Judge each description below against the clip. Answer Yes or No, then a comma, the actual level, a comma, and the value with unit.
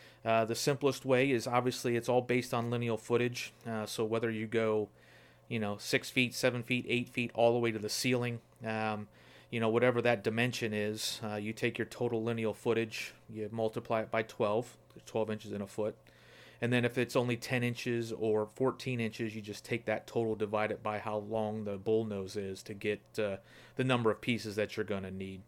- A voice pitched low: Yes, low, 115 Hz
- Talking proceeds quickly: Yes, fast, 210 wpm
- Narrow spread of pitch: Yes, narrow, 2.1 semitones